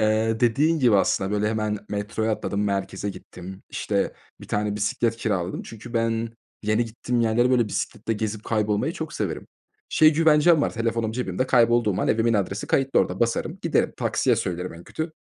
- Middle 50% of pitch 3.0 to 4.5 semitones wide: No, narrow, 2.5 semitones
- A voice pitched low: Yes, low, 110 Hz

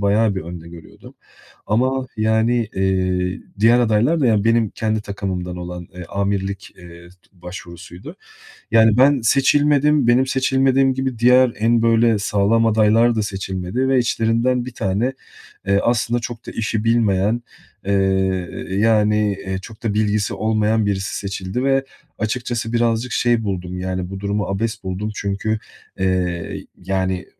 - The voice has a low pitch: Yes, low, 110 Hz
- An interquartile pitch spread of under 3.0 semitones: No, average, 3.7 semitones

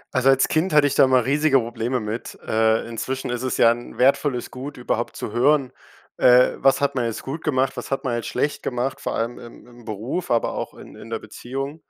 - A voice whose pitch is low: Yes, low, 130 Hz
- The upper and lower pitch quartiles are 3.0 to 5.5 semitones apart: No, narrow, 2.5 semitones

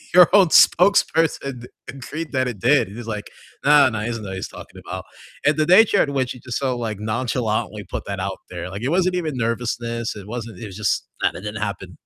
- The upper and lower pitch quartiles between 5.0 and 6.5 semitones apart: Yes, average, 5.3 semitones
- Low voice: Yes, low, 120 Hz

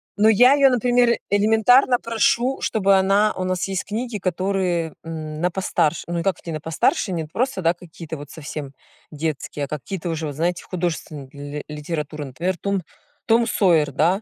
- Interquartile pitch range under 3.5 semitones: No, average, 5.2 semitones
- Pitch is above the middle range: No, medium, 180 Hz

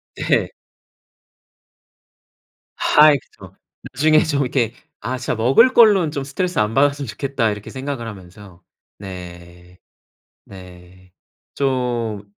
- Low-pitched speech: Yes, low, 120 Hz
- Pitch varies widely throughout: Yes, wide, 6.7 semitones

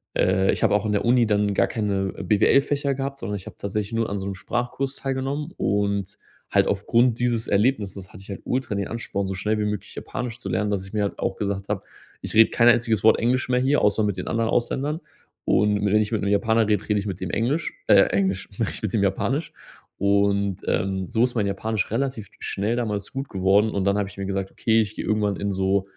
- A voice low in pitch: Yes, low, 105 Hz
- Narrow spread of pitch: No, average, 3.0 semitones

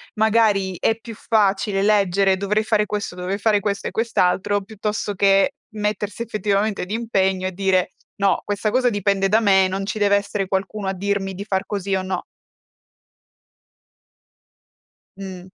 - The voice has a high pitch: Yes, high, 200 Hz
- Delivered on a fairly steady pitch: Yes, narrow, 1.7 semitones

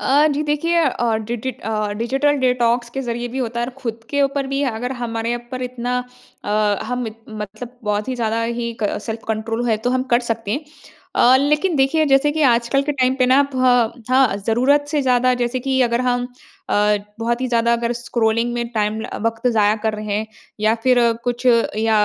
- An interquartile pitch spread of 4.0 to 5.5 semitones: No, narrow, 2.5 semitones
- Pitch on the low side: No, high, 240 Hz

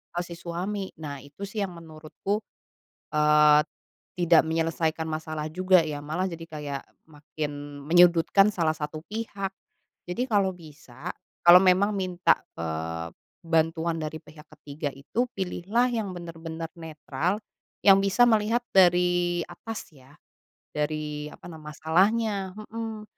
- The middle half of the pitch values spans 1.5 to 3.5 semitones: No, average, 3.9 semitones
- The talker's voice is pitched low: No, medium, 165 Hz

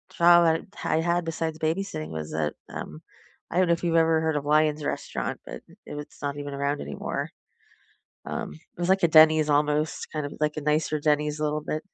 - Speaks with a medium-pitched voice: Yes, medium, 155 Hz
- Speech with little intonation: Yes, narrow, 1.8 semitones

